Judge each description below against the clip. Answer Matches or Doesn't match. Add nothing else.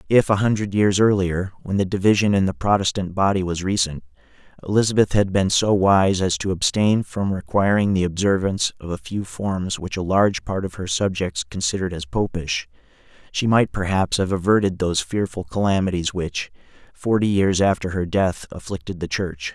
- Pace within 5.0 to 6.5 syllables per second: Matches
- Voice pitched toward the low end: Matches